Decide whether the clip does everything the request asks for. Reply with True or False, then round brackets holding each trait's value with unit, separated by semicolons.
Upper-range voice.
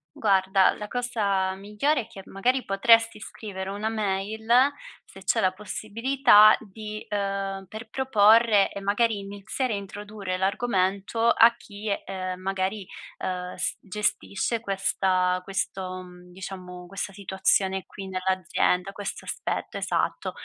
True (195 Hz)